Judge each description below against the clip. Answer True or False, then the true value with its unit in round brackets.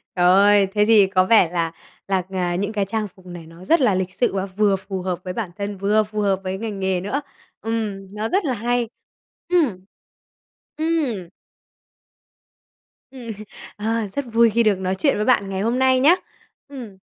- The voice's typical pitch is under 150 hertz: False (205 Hz)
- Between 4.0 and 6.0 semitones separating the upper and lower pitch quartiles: False (3.5 semitones)